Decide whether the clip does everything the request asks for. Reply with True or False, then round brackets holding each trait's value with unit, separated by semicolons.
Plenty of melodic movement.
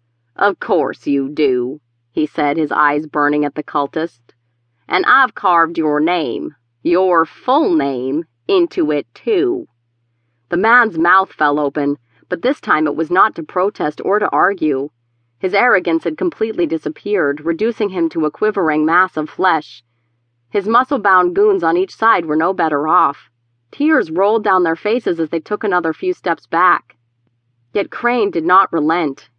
True (7.1 semitones)